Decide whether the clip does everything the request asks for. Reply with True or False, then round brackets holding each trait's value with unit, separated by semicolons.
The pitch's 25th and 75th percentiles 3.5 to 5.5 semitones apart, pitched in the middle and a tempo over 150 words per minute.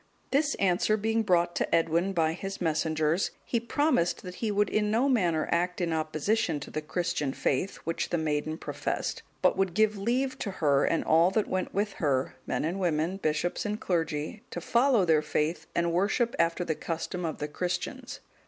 True (4.7 semitones; 175 Hz; 190 wpm)